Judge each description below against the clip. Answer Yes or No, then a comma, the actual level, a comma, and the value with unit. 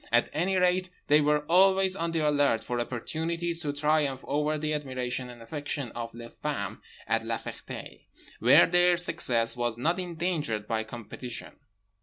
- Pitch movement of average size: No, wide, 5.7 semitones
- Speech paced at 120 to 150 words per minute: No, average, 160 wpm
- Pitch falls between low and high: Yes, medium, 150 Hz